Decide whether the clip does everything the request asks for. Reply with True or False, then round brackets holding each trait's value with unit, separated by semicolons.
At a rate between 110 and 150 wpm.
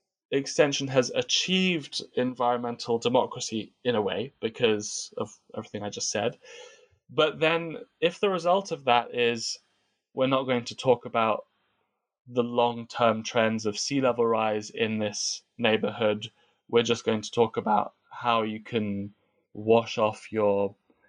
True (145 wpm)